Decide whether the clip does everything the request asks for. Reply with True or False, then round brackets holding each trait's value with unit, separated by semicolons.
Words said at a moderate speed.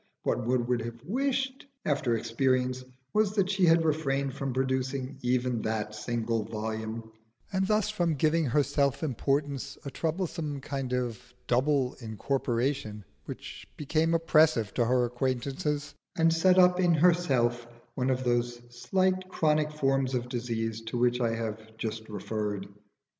True (145 wpm)